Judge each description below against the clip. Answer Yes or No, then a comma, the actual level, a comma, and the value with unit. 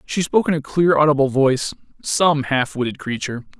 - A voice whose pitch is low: No, medium, 145 Hz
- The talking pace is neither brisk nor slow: Yes, average, 185 wpm